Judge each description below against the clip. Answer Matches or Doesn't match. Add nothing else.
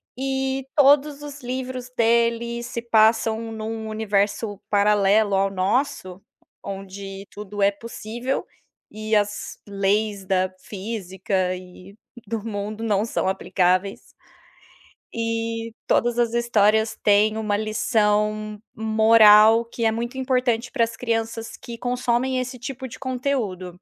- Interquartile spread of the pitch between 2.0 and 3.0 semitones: Matches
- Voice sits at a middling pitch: Doesn't match